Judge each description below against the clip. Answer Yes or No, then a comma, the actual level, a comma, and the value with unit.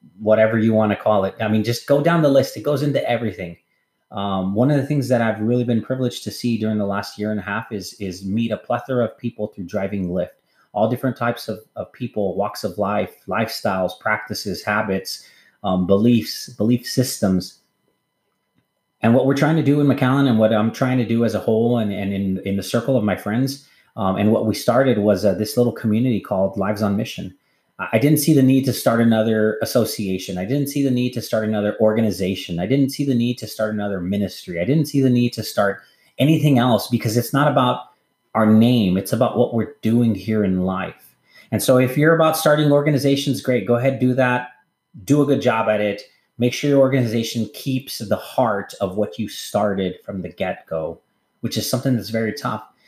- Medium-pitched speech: No, low, 115 Hz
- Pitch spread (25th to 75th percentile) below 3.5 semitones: No, average, 3.8 semitones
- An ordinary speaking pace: No, fast, 215 wpm